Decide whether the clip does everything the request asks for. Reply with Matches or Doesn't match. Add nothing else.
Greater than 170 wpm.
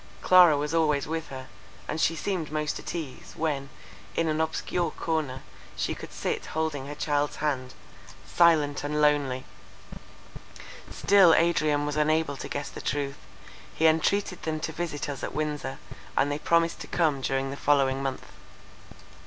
Doesn't match